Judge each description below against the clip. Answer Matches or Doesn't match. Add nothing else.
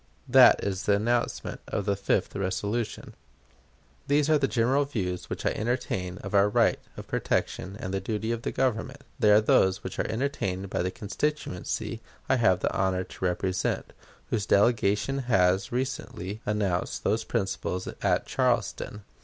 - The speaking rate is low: Doesn't match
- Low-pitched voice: Matches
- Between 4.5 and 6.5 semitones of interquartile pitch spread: Doesn't match